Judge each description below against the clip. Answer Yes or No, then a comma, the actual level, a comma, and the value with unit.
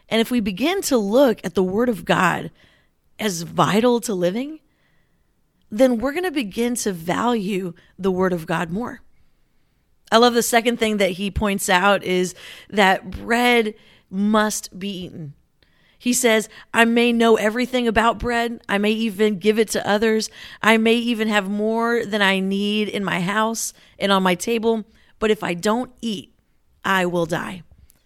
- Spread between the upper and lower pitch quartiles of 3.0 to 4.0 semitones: Yes, average, 3.3 semitones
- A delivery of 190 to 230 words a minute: No, average, 170 wpm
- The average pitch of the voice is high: Yes, high, 215 Hz